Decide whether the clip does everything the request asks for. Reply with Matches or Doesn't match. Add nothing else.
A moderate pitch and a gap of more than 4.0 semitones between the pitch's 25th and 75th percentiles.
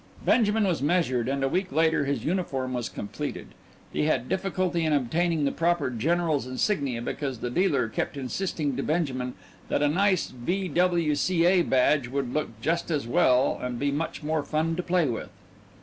Matches